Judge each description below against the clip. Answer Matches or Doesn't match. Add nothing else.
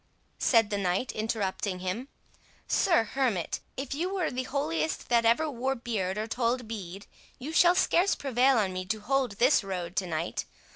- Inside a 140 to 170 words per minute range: Matches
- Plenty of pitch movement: Matches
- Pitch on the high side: Matches